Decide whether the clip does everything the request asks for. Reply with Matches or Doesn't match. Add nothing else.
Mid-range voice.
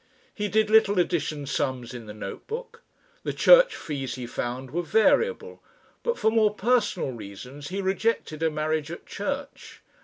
Matches